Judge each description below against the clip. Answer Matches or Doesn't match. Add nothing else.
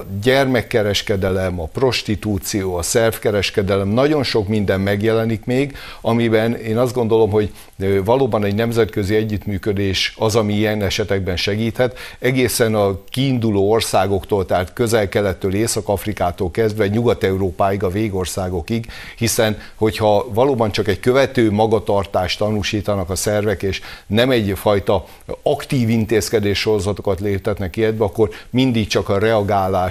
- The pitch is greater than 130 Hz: Doesn't match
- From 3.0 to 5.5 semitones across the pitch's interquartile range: Doesn't match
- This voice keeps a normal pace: Matches